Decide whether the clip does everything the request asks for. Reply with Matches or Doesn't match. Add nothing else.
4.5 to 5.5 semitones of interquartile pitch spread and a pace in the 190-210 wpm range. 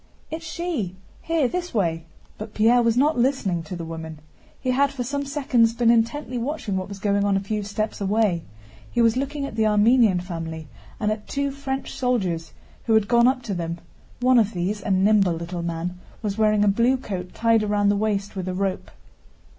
Matches